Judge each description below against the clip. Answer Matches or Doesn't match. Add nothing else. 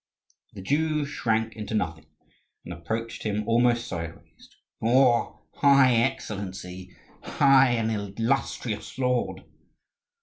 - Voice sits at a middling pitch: Doesn't match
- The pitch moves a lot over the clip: Doesn't match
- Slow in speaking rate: Matches